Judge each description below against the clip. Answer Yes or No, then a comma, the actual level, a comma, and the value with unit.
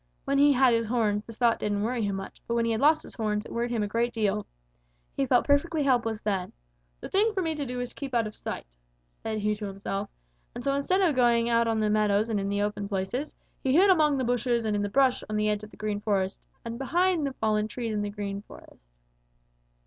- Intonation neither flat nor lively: Yes, average, 4.0 semitones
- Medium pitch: No, high, 230 Hz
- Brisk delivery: Yes, fast, 255 wpm